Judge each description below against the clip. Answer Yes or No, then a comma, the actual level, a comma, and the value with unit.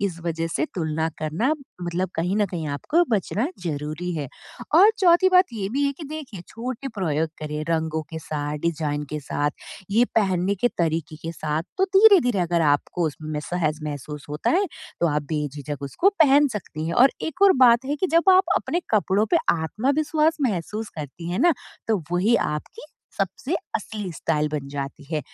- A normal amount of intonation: No, wide, 8.4 semitones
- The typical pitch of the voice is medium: Yes, medium, 175 Hz